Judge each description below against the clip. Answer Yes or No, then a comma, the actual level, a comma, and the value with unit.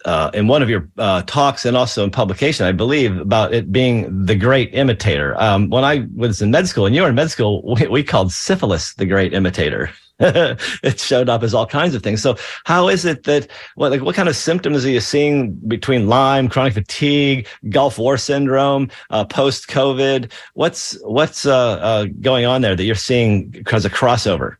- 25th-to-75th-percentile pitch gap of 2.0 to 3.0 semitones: No, average, 4.7 semitones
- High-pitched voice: No, low, 120 Hz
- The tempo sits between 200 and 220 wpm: Yes, fast, 205 wpm